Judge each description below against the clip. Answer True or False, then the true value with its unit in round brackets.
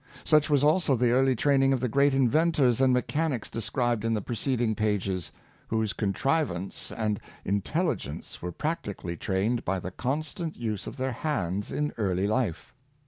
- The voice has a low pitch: True (120 Hz)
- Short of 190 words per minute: True (160 wpm)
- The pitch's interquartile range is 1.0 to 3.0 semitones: False (5.4 semitones)